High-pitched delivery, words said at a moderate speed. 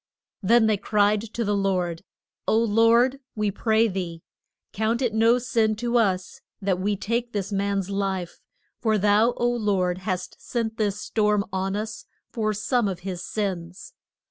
Yes: high, 210 Hz; average, 160 wpm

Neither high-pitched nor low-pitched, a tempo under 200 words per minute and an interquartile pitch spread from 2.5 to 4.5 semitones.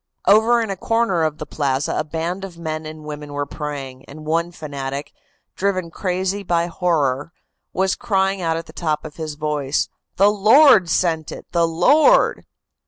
Yes: medium, 165 Hz; average, 170 wpm; average, 4.1 semitones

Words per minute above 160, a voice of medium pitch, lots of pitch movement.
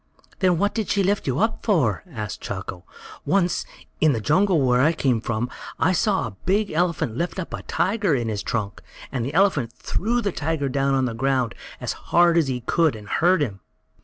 Yes: fast, 205 wpm; medium, 145 Hz; wide, 7.4 semitones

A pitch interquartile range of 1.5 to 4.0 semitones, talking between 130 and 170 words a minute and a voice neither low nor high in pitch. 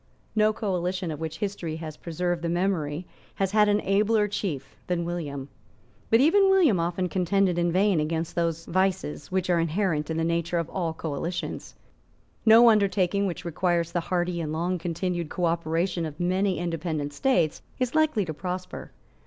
Yes: average, 2.9 semitones; average, 165 wpm; medium, 175 Hz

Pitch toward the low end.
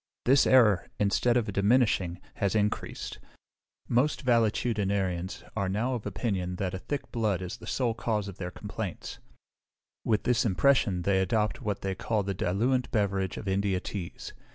Yes: low, 105 Hz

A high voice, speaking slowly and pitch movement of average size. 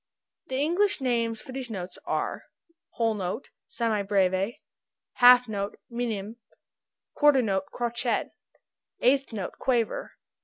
Yes: high, 230 Hz; slow, 115 wpm; average, 3.9 semitones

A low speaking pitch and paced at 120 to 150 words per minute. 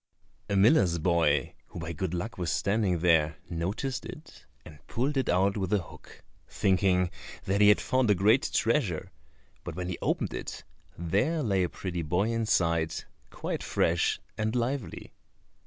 No: very low, 95 Hz; average, 160 wpm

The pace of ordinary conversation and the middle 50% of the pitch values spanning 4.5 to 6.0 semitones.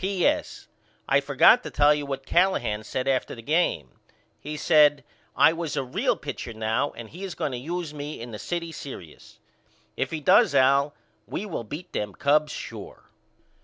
Yes: average, 180 wpm; average, 4.8 semitones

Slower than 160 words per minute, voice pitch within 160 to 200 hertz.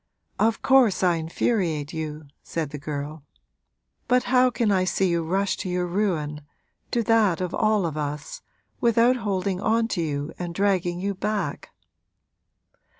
Yes: average, 150 wpm; medium, 185 Hz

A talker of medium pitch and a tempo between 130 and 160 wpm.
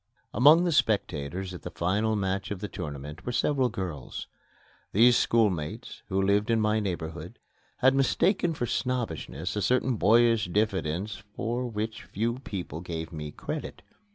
No: low, 105 Hz; average, 150 wpm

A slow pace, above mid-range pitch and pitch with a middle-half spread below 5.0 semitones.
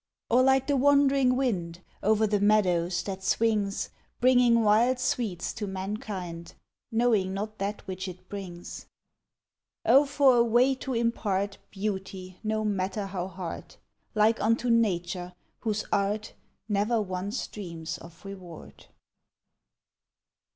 Yes: slow, 125 wpm; high, 205 Hz; average, 3.7 semitones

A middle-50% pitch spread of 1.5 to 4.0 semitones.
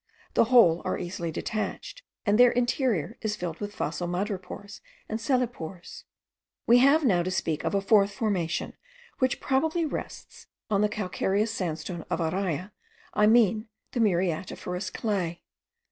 No: average, 4.5 semitones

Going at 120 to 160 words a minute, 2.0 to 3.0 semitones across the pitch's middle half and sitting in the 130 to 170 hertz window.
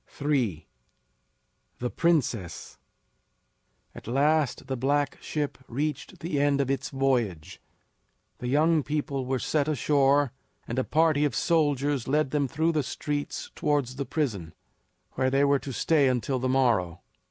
Yes: average, 140 wpm; average, 2.7 semitones; medium, 140 Hz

